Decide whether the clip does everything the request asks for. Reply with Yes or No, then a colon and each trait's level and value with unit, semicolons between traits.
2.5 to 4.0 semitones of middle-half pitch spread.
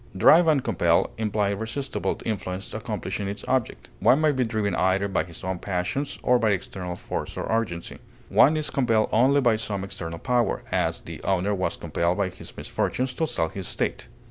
No: average, 5.0 semitones